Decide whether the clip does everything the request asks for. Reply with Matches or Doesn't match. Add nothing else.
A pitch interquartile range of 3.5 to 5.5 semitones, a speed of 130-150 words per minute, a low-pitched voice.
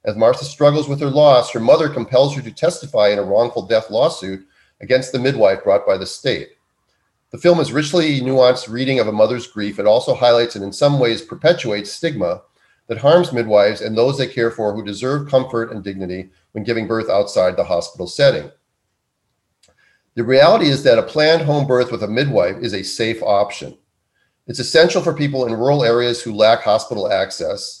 Doesn't match